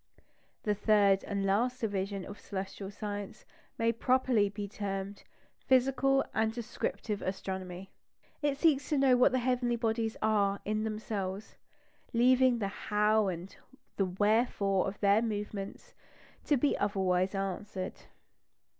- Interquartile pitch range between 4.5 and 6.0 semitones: No, average, 3.2 semitones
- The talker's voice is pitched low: No, high, 210 Hz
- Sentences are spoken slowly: Yes, slow, 130 wpm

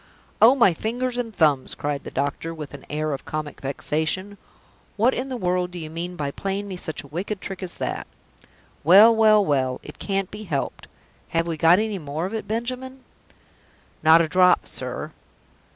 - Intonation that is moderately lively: No, wide, 5.7 semitones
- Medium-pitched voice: Yes, medium, 180 Hz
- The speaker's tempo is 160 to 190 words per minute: Yes, average, 185 wpm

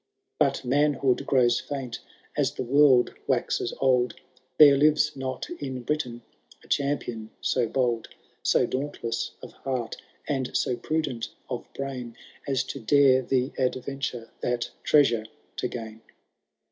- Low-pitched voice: Yes, low, 130 Hz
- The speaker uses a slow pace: Yes, slow, 130 wpm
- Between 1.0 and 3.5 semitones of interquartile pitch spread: Yes, average, 2.7 semitones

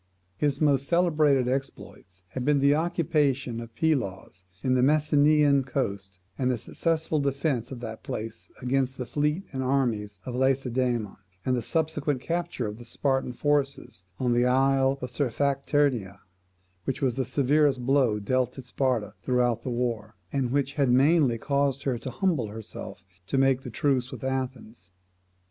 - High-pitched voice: No, low, 130 Hz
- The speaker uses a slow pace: No, average, 155 wpm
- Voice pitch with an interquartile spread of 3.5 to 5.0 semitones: No, average, 2.7 semitones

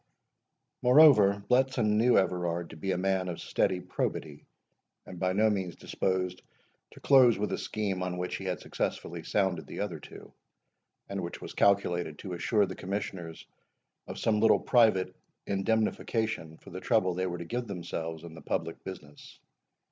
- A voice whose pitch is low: Yes, very low, 95 Hz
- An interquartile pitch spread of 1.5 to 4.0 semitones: Yes, average, 3.4 semitones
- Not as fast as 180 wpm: Yes, average, 165 wpm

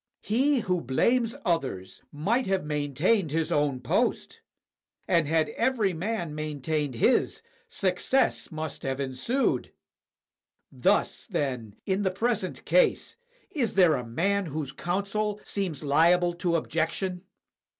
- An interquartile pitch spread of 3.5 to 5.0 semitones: No, wide, 5.6 semitones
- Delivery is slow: Yes, slow, 120 wpm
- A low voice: No, medium, 170 Hz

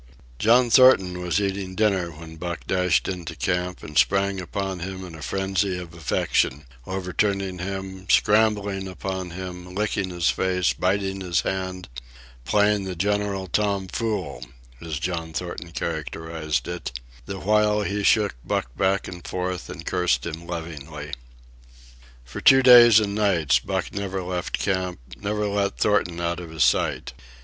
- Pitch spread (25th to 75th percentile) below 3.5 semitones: Yes, average, 2.8 semitones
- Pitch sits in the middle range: No, very low, 95 Hz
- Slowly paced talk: No, average, 145 wpm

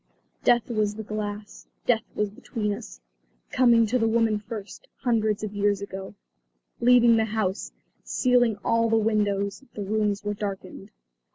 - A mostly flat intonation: Yes, narrow, 2.0 semitones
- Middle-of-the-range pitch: No, high, 215 Hz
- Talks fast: No, average, 150 wpm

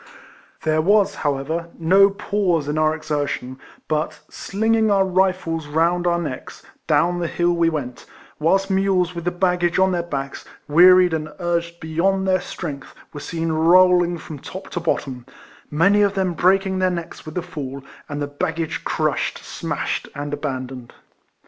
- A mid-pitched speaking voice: Yes, medium, 170 Hz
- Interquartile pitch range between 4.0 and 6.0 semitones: No, average, 3.3 semitones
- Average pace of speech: Yes, average, 160 wpm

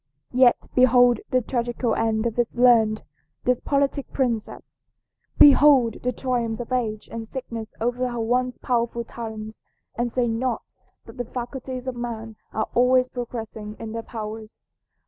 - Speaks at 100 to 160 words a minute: Yes, average, 145 wpm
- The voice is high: Yes, high, 240 Hz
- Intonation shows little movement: Yes, narrow, 2.0 semitones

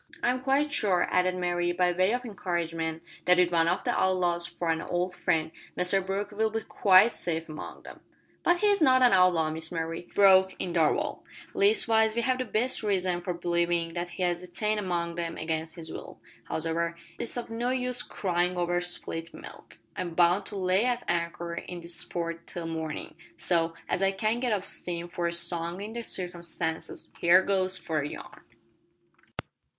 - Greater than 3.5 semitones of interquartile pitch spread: No, average, 3.2 semitones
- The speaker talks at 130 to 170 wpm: No, average, 185 wpm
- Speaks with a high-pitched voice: No, medium, 180 Hz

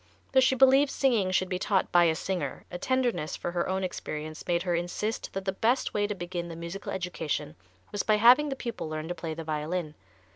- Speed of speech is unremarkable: No, fast, 220 wpm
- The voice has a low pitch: No, medium, 185 Hz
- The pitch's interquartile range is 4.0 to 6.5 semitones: Yes, average, 4.5 semitones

